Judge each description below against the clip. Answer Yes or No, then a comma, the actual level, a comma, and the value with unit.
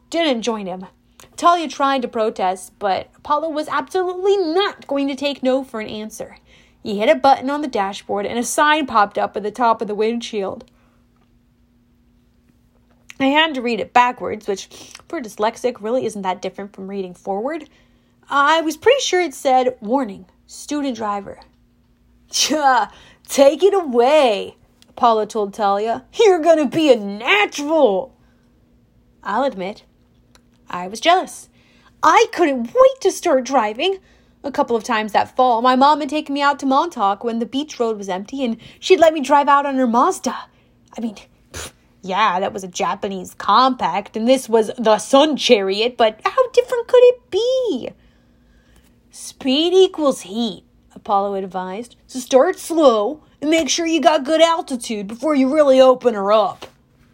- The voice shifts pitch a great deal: Yes, wide, 6.3 semitones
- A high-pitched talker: Yes, very high, 255 Hz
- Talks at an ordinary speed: Yes, average, 160 wpm